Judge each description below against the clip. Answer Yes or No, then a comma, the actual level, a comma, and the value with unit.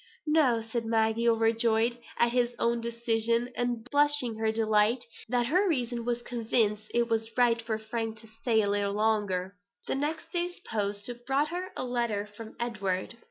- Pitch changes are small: Yes, narrow, 1.9 semitones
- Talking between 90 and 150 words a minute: No, average, 165 wpm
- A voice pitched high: Yes, high, 230 Hz